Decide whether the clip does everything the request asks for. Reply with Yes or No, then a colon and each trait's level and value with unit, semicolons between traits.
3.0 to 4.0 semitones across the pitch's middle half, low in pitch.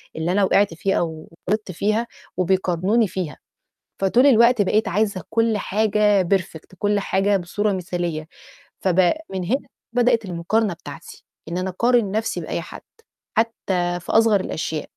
No: average, 3.6 semitones; high, 195 Hz